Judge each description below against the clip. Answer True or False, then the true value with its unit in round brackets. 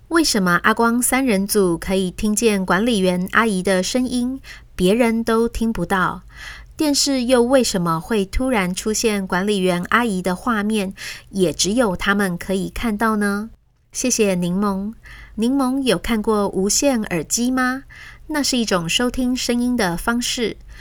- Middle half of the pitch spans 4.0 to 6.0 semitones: True (4.5 semitones)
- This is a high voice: True (215 Hz)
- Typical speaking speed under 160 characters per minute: False (230 characters per minute)